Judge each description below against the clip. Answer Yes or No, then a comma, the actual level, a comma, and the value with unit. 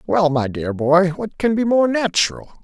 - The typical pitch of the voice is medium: Yes, medium, 175 Hz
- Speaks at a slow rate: No, fast, 205 wpm